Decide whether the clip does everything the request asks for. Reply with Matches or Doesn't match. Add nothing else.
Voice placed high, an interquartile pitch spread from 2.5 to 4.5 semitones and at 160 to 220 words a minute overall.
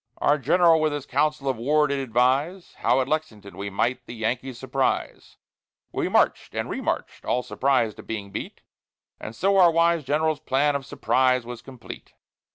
Doesn't match